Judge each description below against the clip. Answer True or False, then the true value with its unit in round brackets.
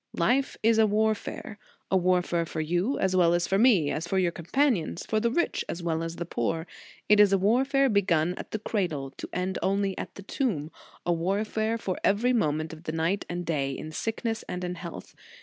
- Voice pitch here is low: False (185 Hz)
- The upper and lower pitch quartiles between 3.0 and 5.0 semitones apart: True (4.5 semitones)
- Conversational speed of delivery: False (215 wpm)